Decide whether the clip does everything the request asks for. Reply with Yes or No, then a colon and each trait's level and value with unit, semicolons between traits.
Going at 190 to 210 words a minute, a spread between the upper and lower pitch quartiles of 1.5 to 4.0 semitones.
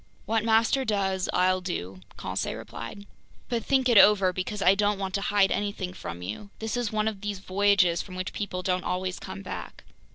Yes: average, 195 wpm; narrow, 2.4 semitones